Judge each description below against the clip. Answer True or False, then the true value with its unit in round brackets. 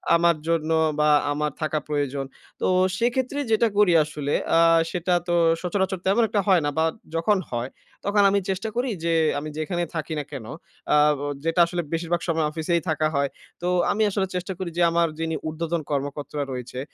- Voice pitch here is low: False (165 Hz)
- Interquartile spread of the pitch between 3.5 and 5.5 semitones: True (3.9 semitones)